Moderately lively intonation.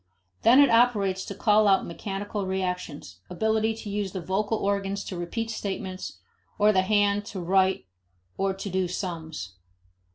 No: narrow, 2.1 semitones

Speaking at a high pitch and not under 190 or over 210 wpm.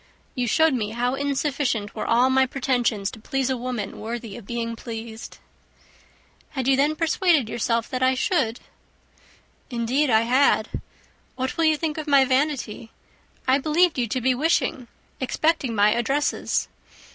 No: very high, 255 Hz; average, 155 wpm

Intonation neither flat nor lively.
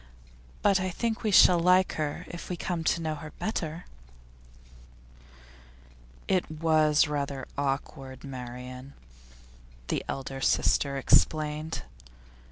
Yes: average, 4.0 semitones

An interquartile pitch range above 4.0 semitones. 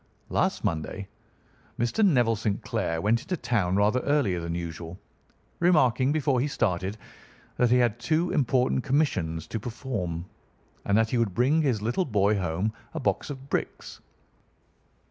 Yes: wide, 5.6 semitones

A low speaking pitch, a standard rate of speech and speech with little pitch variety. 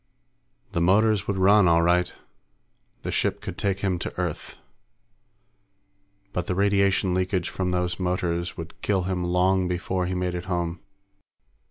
Yes: very low, 90 Hz; average, 150 wpm; narrow, 1.4 semitones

